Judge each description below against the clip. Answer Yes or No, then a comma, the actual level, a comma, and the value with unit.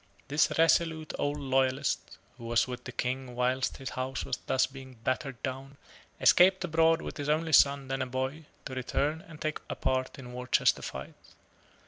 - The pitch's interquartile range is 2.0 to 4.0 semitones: Yes, average, 3.0 semitones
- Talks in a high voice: No, low, 135 Hz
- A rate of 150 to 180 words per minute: Yes, average, 175 wpm